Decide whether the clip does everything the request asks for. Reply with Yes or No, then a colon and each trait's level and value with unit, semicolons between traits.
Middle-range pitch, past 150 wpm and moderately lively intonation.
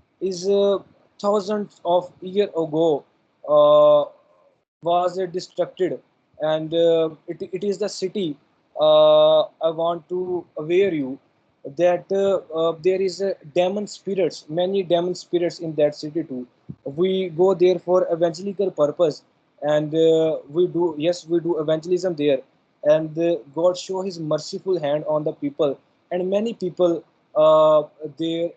No: medium, 175 Hz; average, 145 wpm; average, 3.0 semitones